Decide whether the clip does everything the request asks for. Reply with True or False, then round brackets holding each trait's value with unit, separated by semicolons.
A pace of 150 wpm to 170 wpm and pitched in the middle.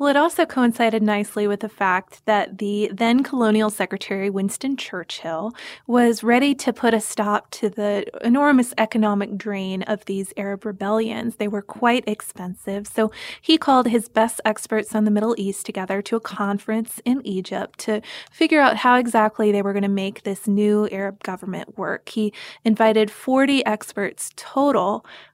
False (165 wpm; 215 Hz)